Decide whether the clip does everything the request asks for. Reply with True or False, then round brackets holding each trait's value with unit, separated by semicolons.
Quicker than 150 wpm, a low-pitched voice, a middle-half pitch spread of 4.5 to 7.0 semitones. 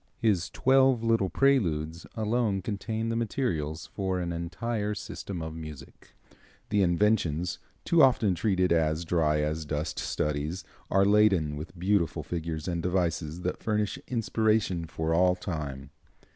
False (135 wpm; 90 Hz; 4.9 semitones)